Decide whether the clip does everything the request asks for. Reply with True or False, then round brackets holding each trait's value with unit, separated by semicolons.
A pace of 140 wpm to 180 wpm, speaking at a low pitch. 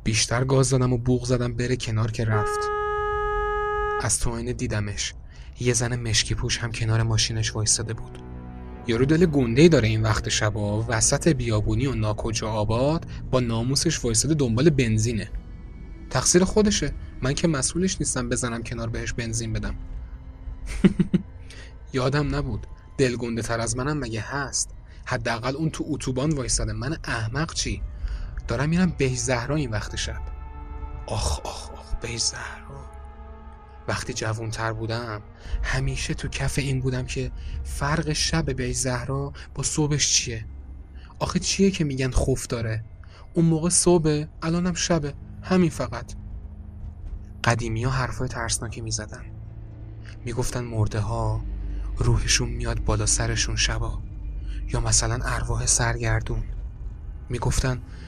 False (130 wpm; 115 Hz)